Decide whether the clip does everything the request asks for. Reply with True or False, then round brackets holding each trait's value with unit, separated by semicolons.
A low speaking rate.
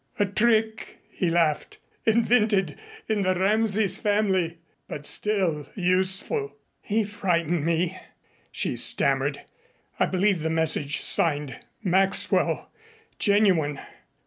True (100 wpm)